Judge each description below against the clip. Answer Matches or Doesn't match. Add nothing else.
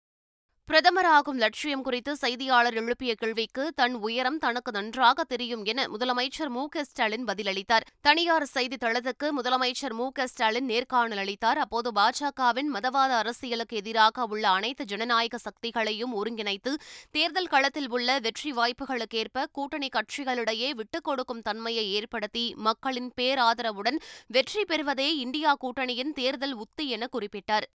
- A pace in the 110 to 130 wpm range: Matches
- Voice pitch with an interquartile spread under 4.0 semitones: Matches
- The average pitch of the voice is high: Matches